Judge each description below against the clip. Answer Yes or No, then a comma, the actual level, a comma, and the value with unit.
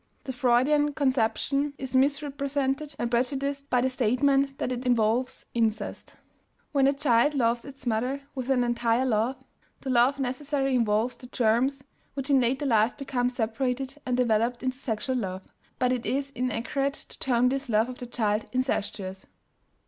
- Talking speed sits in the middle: Yes, average, 160 wpm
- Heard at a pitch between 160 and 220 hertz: No, very high, 255 Hz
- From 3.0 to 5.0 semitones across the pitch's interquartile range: No, narrow, 2.6 semitones